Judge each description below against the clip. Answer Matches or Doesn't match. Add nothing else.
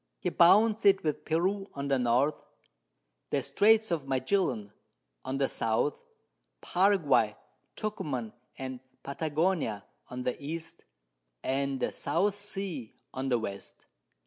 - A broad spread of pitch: Matches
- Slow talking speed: Matches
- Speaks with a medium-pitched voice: Matches